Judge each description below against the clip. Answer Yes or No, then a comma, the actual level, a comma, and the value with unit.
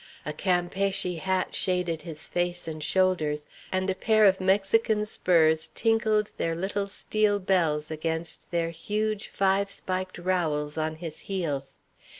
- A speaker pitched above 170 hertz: Yes, medium, 185 Hz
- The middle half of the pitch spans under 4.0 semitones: Yes, average, 3.4 semitones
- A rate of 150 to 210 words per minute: No, average, 140 wpm